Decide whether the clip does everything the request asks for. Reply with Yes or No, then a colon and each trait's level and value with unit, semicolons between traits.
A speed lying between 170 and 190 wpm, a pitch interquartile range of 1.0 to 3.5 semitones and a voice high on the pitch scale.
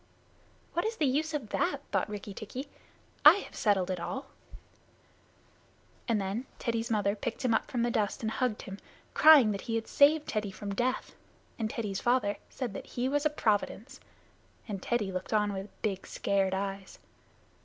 No: average, 175 wpm; average, 4.4 semitones; high, 220 Hz